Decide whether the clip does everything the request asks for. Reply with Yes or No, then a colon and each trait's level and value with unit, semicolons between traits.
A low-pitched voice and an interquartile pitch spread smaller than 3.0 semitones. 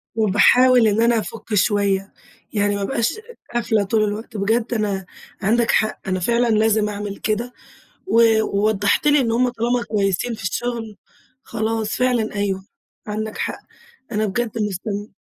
No: high, 215 Hz; narrow, 2.4 semitones